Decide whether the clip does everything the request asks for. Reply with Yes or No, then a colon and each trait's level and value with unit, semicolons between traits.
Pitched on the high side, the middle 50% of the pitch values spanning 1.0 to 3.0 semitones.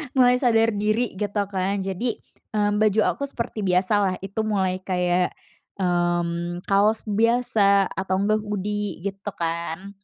Yes: high, 200 Hz; narrow, 2.6 semitones